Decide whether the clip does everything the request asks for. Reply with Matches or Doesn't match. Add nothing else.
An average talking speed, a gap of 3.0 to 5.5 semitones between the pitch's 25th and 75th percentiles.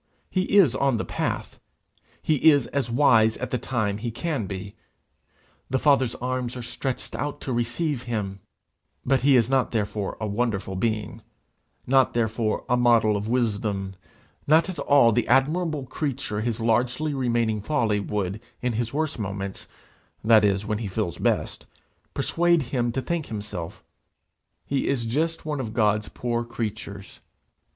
Matches